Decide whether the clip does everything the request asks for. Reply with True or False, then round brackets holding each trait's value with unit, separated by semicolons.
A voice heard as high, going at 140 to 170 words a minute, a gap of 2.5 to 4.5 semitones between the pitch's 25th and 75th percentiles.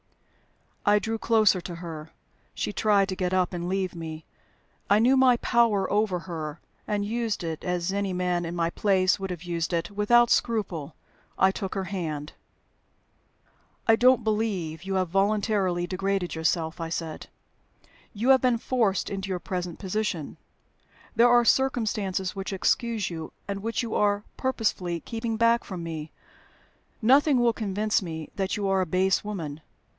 True (195 Hz; 160 wpm; 3.8 semitones)